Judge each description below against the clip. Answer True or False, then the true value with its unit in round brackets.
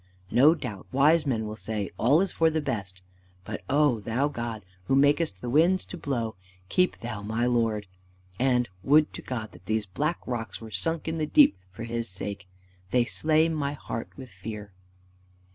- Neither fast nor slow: True (180 wpm)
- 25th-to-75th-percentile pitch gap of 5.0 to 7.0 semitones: True (5.6 semitones)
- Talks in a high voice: False (120 Hz)